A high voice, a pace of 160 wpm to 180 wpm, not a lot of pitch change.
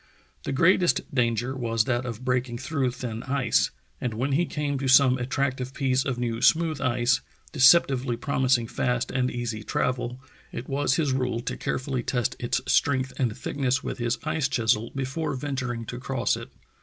No: low, 130 Hz; average, 175 wpm; narrow, 2.1 semitones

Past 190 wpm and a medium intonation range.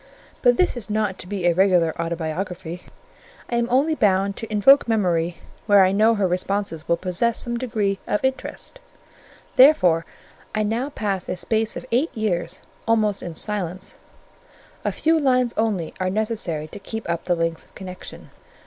No: average, 165 wpm; average, 4.3 semitones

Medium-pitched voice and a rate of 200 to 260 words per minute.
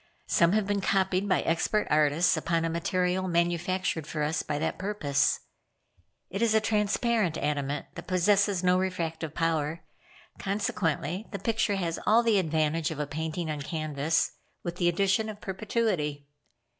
No: medium, 175 Hz; average, 155 wpm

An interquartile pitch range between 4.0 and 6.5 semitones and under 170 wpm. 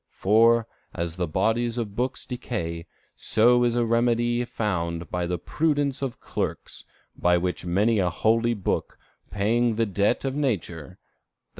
Yes: average, 5.0 semitones; average, 150 wpm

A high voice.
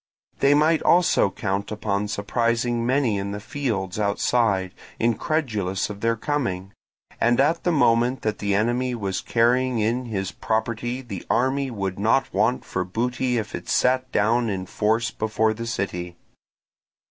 No: low, 115 Hz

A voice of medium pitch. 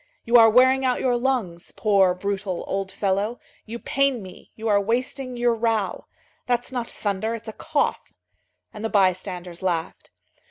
No: high, 220 Hz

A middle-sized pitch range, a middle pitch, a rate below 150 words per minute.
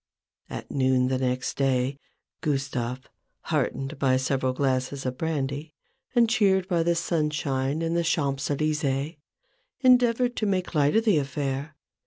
Yes: average, 4.0 semitones; medium, 145 Hz; average, 140 wpm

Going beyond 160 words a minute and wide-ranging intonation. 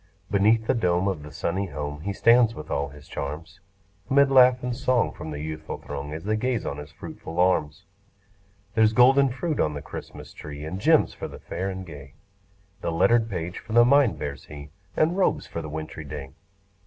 Yes: average, 200 wpm; wide, 7.9 semitones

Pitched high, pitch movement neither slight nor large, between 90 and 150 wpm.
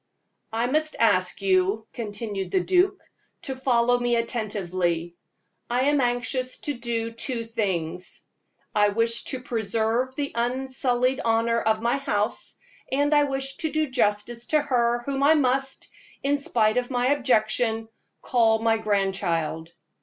Yes: high, 235 Hz; average, 3.4 semitones; average, 140 wpm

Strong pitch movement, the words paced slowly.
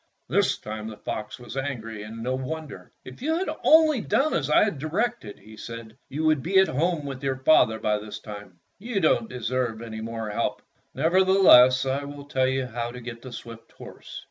No: wide, 5.8 semitones; average, 195 wpm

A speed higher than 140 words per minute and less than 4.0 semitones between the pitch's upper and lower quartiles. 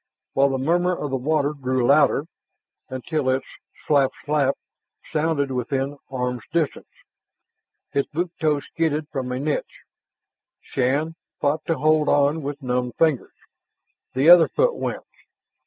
No: slow, 135 wpm; average, 2.9 semitones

